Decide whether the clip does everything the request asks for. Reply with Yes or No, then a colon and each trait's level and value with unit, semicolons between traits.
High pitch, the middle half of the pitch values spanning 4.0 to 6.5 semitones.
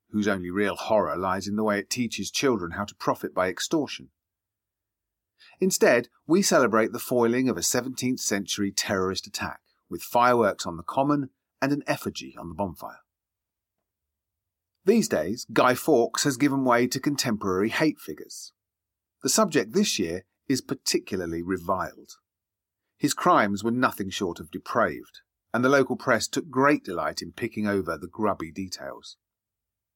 No: low, 105 Hz; average, 4.8 semitones